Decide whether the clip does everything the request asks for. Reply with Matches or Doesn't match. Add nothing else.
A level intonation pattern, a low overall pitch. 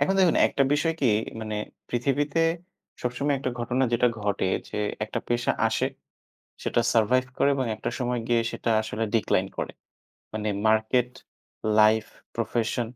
Doesn't match